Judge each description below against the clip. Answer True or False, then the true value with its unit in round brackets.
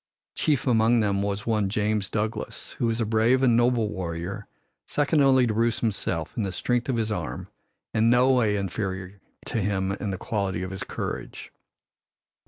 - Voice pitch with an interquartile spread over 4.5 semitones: False (3.2 semitones)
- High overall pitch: False (110 Hz)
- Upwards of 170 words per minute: True (180 wpm)